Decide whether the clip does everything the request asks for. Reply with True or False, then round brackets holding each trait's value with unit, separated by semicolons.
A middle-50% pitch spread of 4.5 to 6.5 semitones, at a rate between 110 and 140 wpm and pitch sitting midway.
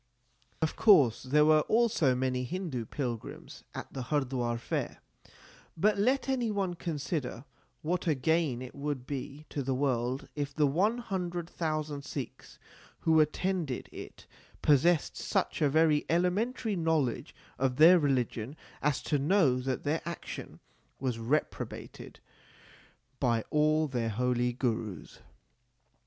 True (4.9 semitones; 135 wpm; 150 Hz)